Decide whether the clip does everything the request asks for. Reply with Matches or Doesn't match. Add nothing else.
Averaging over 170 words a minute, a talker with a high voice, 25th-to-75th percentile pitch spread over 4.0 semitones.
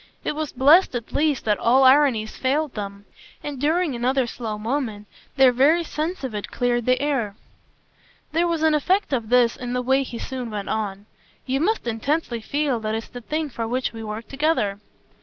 Matches